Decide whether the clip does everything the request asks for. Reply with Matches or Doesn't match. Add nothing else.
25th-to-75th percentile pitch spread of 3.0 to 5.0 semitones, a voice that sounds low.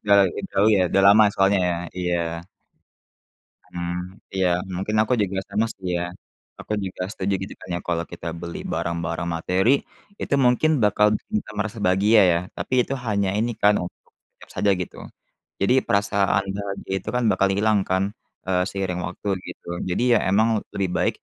Doesn't match